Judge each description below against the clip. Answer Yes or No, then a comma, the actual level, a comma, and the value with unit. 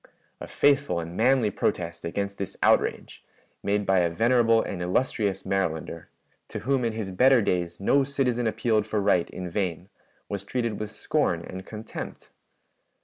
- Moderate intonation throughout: Yes, average, 4.3 semitones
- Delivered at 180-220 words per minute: No, average, 155 wpm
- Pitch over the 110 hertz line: No, low, 105 Hz